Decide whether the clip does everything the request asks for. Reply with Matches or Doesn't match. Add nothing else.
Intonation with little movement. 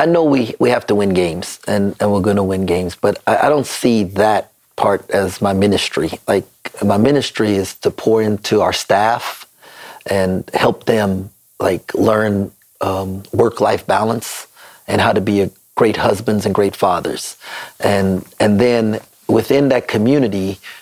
Matches